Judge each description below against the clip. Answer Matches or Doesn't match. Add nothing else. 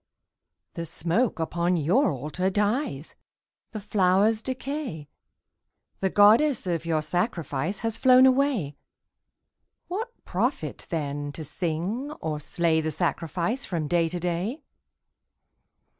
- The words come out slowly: Matches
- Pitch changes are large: Matches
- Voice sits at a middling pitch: Matches